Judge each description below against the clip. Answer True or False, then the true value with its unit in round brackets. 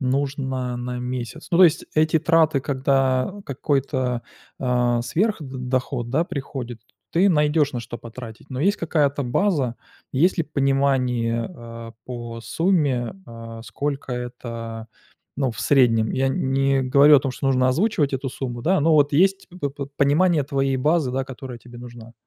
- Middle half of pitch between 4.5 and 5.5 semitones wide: False (3.3 semitones)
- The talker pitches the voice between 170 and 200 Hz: False (135 Hz)